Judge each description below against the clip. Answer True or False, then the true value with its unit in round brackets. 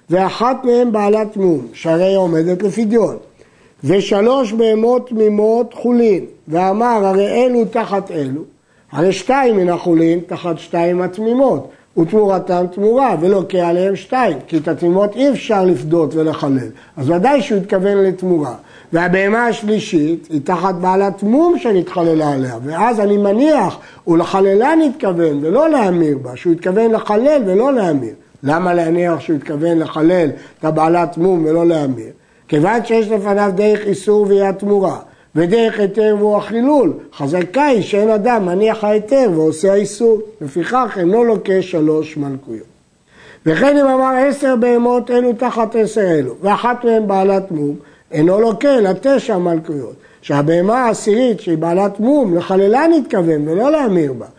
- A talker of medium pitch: False (195 Hz)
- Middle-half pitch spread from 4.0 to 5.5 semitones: True (5.2 semitones)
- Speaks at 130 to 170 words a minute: True (140 wpm)